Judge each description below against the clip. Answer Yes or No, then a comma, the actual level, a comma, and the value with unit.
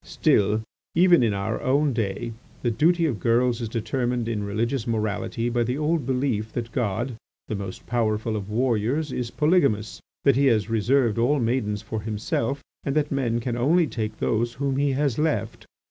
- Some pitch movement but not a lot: Yes, average, 3.9 semitones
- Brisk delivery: No, average, 175 wpm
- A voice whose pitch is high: No, low, 120 Hz